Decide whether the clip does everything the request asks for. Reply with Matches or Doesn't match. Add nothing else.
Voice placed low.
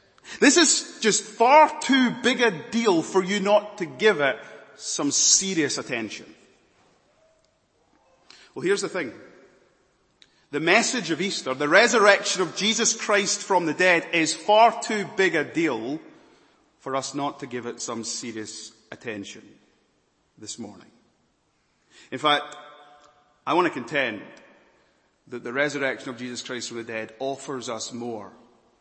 Doesn't match